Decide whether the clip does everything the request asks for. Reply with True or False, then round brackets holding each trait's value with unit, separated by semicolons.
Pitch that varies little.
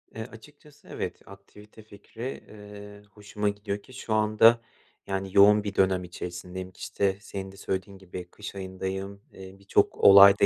True (1.6 semitones)